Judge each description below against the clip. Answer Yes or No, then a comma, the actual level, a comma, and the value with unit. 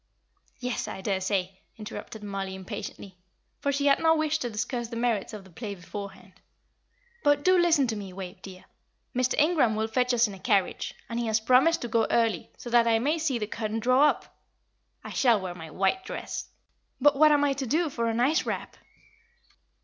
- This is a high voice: Yes, high, 230 Hz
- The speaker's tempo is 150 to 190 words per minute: No, average, 200 wpm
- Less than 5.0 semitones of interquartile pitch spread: No, wide, 5.5 semitones